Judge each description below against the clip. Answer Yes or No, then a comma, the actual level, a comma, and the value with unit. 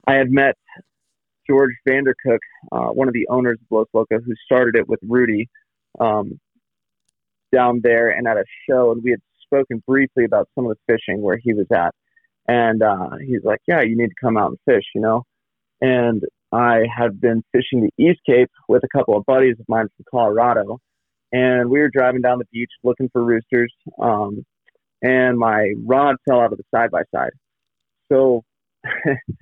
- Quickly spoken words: No, average, 185 wpm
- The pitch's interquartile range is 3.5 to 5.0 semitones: No, narrow, 2.4 semitones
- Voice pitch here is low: Yes, low, 120 Hz